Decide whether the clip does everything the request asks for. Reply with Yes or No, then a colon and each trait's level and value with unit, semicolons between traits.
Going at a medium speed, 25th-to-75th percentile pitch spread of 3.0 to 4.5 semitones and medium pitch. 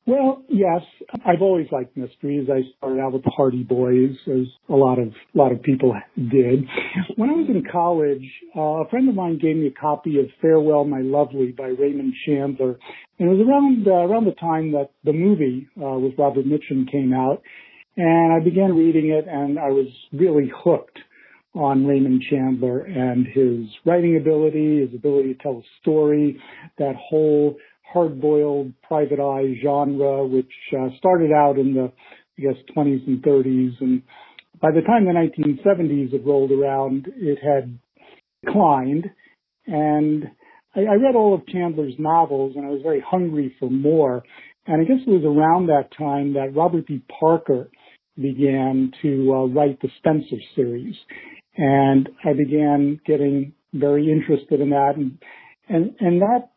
Yes: average, 165 wpm; average, 3.6 semitones; medium, 145 Hz